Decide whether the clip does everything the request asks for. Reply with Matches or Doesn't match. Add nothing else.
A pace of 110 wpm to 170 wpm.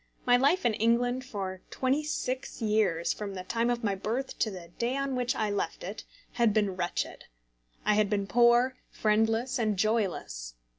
Doesn't match